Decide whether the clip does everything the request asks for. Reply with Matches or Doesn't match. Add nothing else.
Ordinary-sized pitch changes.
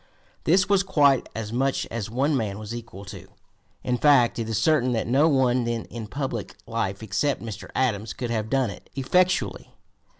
Matches